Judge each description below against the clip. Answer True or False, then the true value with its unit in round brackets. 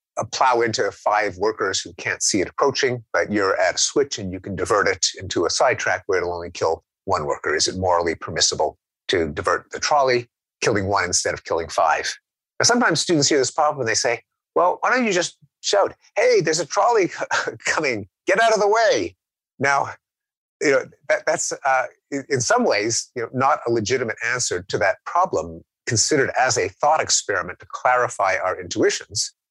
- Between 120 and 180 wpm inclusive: False (195 wpm)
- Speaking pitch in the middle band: True (150 Hz)